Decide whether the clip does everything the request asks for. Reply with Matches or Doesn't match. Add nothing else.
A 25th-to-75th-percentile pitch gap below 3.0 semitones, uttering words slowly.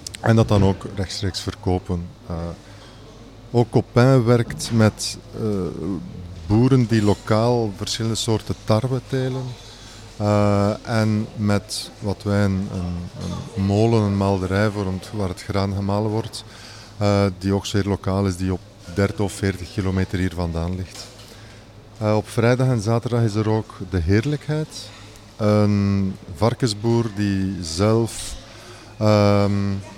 Matches